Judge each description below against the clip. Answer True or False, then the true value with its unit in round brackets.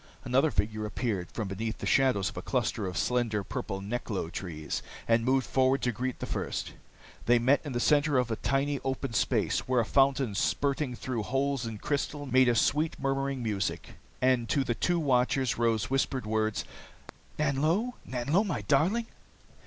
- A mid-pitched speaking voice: False (125 Hz)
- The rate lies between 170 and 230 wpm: True (175 wpm)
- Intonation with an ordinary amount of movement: True (3.6 semitones)